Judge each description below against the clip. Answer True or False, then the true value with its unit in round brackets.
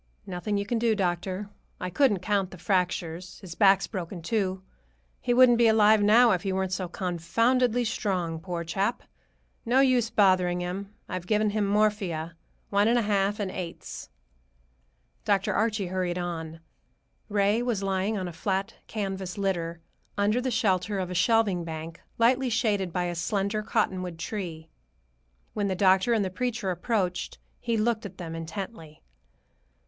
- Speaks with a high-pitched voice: True (195 Hz)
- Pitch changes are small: False (3.2 semitones)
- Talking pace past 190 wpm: False (160 wpm)